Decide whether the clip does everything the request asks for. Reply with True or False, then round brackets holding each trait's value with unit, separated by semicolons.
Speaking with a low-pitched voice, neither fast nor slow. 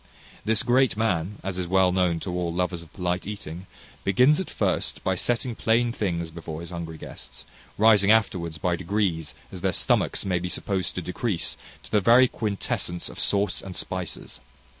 True (95 Hz; 180 wpm)